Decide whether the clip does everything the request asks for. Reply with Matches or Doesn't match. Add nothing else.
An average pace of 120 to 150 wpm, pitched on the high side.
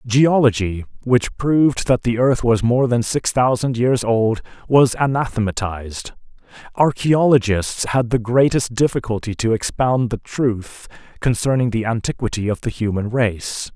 Doesn't match